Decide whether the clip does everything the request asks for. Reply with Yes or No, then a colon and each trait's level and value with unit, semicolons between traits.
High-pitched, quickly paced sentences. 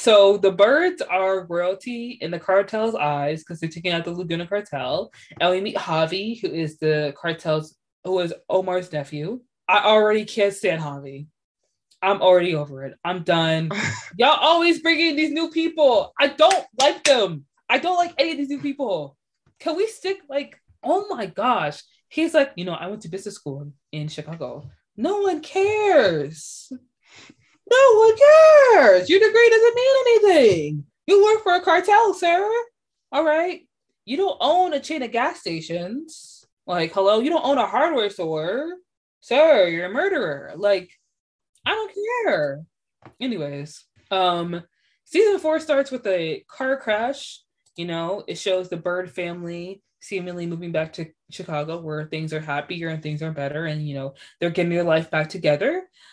No: high, 200 Hz; average, 165 wpm